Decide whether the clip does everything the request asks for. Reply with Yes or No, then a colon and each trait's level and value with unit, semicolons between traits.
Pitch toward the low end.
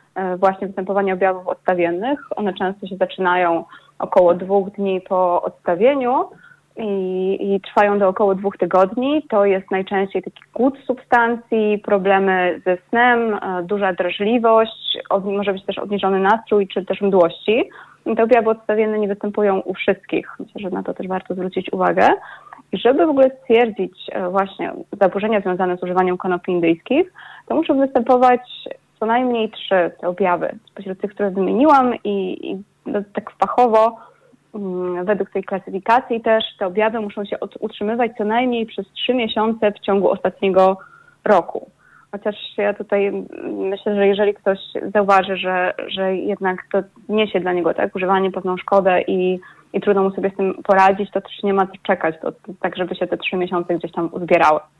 No: high, 200 Hz